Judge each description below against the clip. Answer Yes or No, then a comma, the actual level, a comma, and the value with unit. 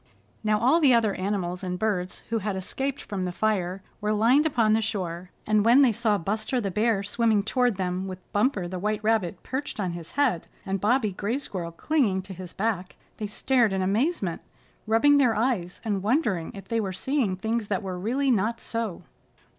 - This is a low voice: No, high, 210 Hz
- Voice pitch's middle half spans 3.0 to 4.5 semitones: Yes, average, 3.8 semitones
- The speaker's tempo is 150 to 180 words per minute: No, average, 195 wpm